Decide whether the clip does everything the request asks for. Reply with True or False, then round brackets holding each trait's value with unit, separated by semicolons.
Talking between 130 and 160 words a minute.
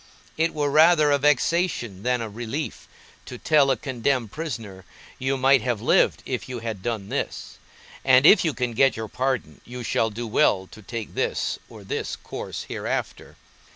False (175 wpm)